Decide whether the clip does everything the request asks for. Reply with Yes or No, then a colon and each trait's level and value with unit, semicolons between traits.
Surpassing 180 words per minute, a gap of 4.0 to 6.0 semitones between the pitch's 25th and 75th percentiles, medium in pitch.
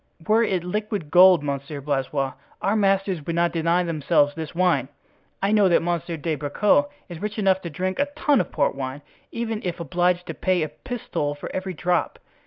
Yes: average, 190 wpm; average, 4.5 semitones; medium, 175 Hz